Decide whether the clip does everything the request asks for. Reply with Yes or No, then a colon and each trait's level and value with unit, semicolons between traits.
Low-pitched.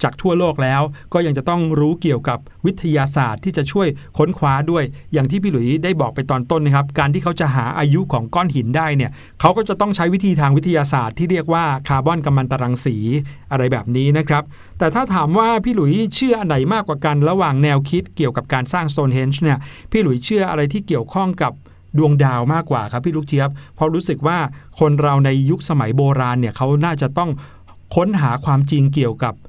No: medium, 150 Hz